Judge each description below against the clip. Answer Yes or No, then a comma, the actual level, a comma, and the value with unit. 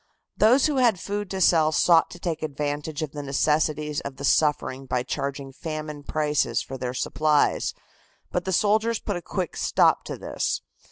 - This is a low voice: No, medium, 155 Hz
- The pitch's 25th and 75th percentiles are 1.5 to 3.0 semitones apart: No, average, 3.9 semitones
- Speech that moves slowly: No, average, 175 wpm